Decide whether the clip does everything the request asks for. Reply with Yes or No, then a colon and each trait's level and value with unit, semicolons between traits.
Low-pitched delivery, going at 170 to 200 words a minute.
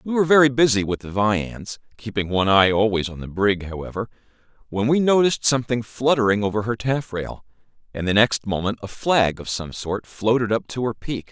Yes: low, 110 Hz; average, 195 wpm